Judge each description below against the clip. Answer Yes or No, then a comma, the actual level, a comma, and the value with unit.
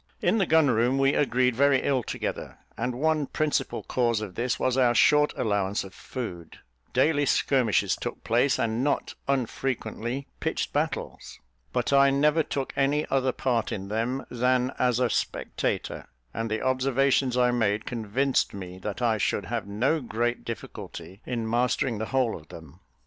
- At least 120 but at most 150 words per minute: No, average, 165 wpm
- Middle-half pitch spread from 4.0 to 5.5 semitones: No, average, 3.5 semitones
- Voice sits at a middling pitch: No, low, 125 Hz